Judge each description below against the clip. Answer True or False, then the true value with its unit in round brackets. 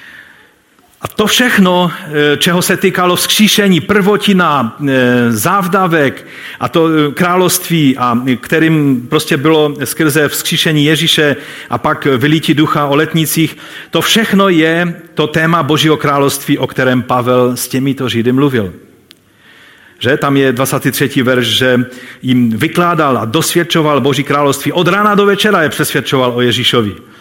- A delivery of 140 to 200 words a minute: False (130 wpm)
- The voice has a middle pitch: True (150 Hz)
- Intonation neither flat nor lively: True (4.7 semitones)